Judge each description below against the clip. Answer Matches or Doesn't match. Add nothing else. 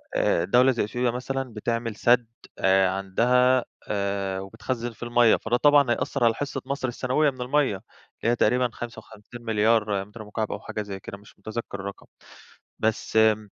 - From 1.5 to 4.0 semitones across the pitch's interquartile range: Matches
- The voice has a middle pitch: Doesn't match